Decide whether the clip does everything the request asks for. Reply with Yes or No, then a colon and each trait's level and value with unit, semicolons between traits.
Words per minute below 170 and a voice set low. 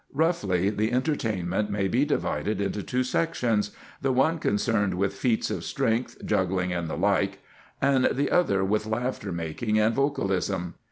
Yes: average, 155 wpm; low, 105 Hz